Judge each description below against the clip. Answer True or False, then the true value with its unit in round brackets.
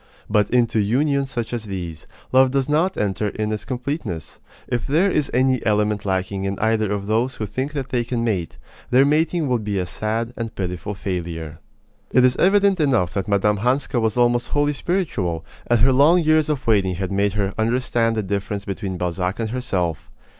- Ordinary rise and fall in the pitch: True (5.0 semitones)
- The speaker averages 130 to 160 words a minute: False (190 wpm)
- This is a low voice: True (115 Hz)